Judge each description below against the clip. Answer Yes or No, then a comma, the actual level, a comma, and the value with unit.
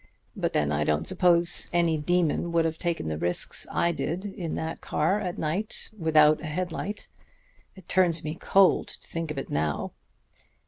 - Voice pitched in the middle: Yes, medium, 165 Hz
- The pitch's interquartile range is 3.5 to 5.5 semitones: No, narrow, 2.6 semitones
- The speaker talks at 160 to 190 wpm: Yes, average, 180 wpm